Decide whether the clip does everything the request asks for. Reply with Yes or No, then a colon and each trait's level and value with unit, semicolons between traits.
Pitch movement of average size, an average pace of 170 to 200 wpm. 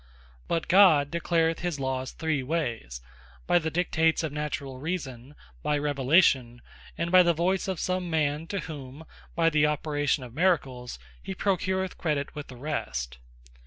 No: average, 4.1 semitones; average, 155 wpm